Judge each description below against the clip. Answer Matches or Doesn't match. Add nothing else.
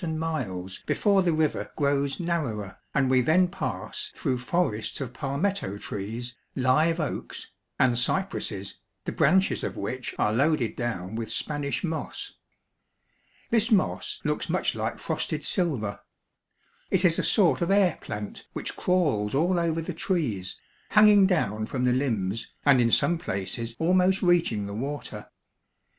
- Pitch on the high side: Doesn't match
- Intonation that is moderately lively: Doesn't match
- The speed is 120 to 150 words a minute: Matches